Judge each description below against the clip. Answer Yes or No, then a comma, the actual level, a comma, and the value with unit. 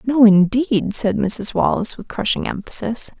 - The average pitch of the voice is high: Yes, high, 220 Hz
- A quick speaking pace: No, average, 150 wpm